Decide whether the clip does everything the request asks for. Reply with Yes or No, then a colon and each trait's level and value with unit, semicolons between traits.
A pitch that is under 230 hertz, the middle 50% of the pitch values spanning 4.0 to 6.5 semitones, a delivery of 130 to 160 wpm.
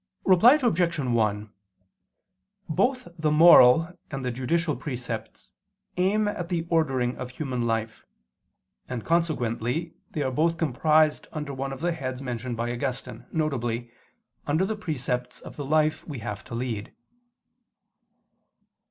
Yes: medium, 140 Hz; average, 5.2 semitones; slow, 135 wpm